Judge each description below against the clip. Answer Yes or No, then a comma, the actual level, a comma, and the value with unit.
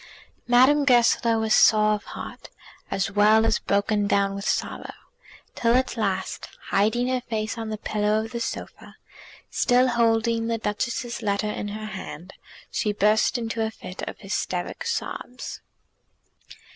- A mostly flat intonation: Yes, narrow, 2.3 semitones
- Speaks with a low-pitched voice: No, high, 220 Hz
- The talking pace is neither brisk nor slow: Yes, average, 145 wpm